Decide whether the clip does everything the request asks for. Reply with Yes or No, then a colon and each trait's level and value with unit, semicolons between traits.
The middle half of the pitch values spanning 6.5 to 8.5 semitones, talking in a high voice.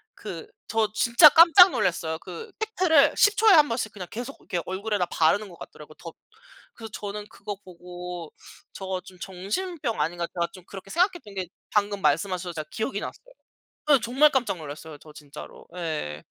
Yes: wide, 7.3 semitones; high, 200 Hz